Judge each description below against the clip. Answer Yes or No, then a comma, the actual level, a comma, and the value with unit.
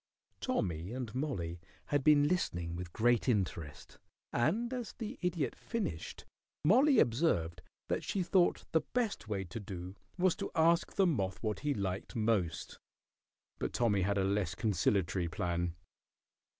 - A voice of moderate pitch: No, low, 110 Hz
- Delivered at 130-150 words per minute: Yes, average, 145 wpm